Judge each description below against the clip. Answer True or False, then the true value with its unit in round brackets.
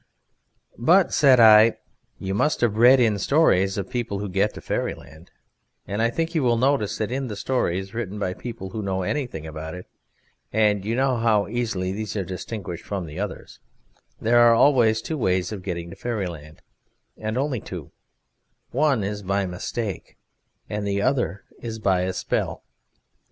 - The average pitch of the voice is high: False (105 Hz)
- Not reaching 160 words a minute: False (170 wpm)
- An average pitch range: True (4.0 semitones)